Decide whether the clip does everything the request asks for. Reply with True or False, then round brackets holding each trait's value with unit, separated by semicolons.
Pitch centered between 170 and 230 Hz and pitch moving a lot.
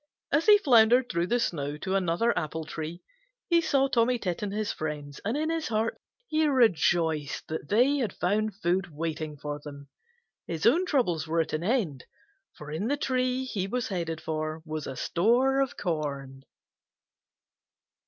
True (185 Hz; 8.0 semitones)